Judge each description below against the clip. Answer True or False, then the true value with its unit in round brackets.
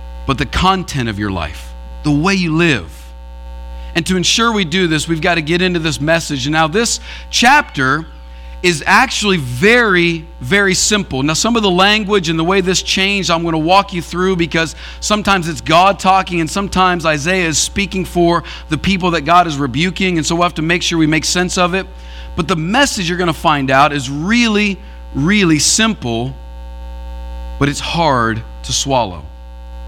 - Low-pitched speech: False (170 Hz)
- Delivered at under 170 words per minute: False (190 wpm)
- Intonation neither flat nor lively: False (8.2 semitones)